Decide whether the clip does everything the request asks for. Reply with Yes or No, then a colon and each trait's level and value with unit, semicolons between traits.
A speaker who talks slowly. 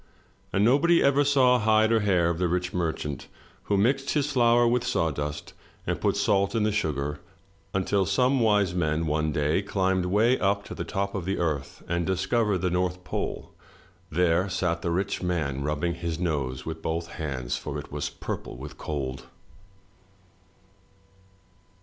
No: average, 165 wpm